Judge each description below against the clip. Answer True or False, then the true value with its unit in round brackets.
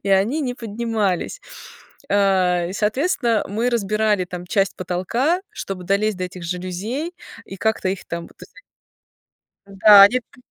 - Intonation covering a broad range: False (4.0 semitones)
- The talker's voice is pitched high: True (200 Hz)